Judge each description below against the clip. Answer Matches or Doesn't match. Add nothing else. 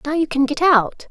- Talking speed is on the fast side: Matches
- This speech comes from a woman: Matches